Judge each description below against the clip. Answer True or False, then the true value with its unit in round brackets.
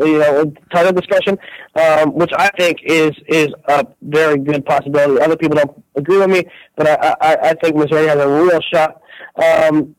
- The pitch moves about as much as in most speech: False (2.0 semitones)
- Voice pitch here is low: False (155 Hz)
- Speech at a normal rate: True (185 wpm)